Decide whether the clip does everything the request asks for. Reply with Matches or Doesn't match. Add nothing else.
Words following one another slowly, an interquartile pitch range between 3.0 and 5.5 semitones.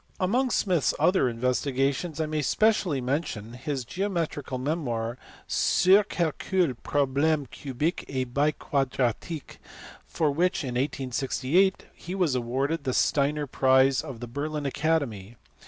Matches